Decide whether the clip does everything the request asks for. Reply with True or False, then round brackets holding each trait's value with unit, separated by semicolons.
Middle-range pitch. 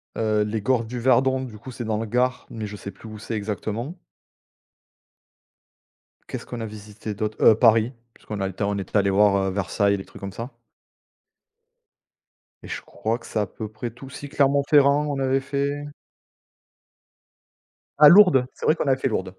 False (115 Hz)